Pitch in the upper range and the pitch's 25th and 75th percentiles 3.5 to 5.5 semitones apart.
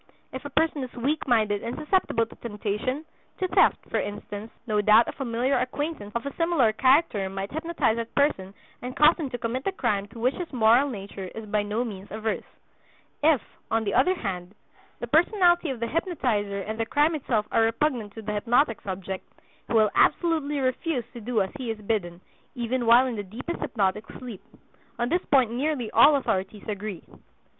Yes: high, 235 Hz; average, 5.2 semitones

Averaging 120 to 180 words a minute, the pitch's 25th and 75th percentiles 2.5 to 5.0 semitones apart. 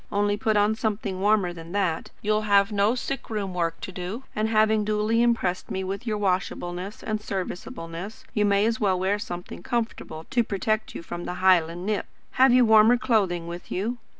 No: average, 195 wpm; average, 3.1 semitones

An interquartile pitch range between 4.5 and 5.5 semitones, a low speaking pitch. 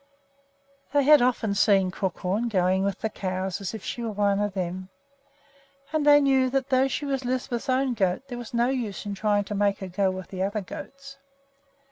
No: average, 5.2 semitones; high, 210 Hz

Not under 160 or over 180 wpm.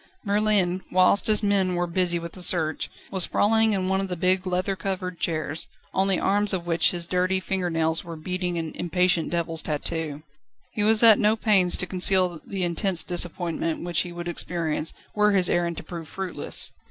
No: average, 190 wpm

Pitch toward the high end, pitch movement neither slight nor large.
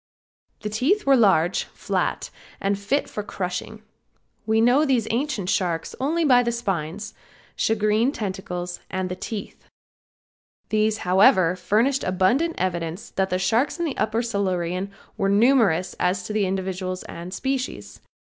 Yes: high, 205 Hz; average, 4.4 semitones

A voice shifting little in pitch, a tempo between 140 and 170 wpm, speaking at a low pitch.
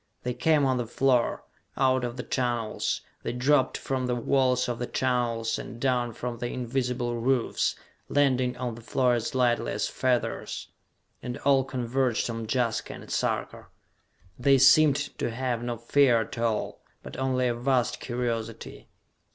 Yes: narrow, 1.7 semitones; average, 160 wpm; low, 125 Hz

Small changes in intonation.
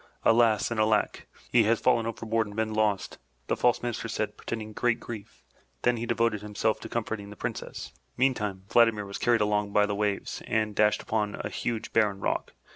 Yes: narrow, 1.8 semitones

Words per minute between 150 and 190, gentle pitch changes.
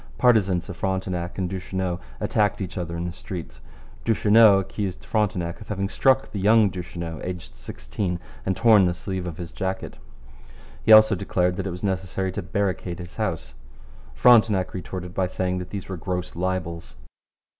Yes: average, 165 wpm; narrow, 2.2 semitones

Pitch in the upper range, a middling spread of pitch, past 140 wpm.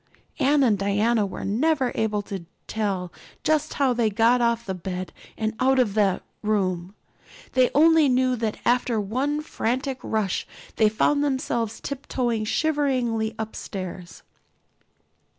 No: high, 230 Hz; average, 4.1 semitones; slow, 135 wpm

